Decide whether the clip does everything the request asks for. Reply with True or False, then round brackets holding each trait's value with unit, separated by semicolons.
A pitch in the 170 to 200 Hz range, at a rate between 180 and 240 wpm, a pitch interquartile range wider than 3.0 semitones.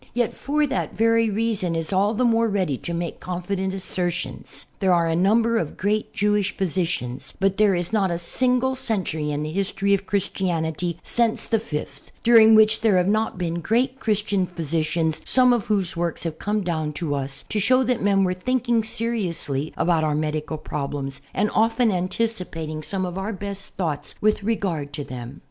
True (190 Hz; 185 wpm; 5.0 semitones)